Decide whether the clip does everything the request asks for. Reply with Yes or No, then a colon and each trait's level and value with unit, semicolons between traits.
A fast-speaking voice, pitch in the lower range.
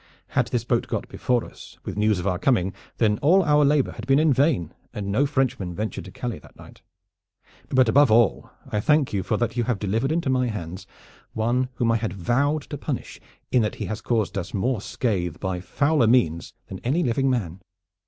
Yes: fast, 210 wpm; low, 115 Hz